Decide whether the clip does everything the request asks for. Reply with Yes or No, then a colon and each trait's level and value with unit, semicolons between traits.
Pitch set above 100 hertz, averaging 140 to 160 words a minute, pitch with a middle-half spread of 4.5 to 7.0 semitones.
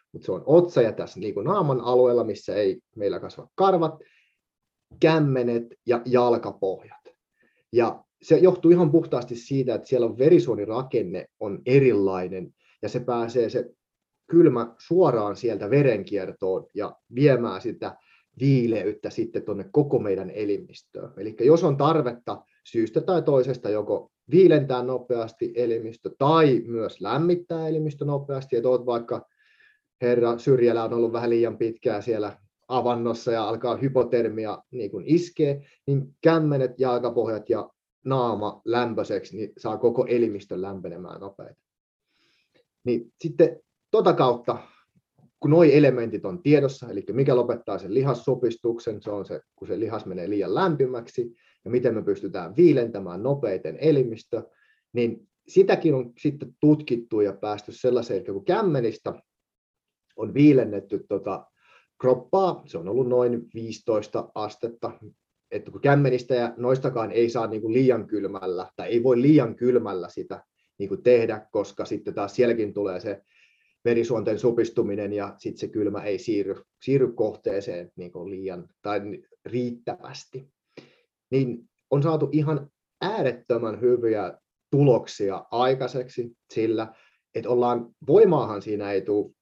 No: low, 125 Hz; average, 130 wpm; average, 4.8 semitones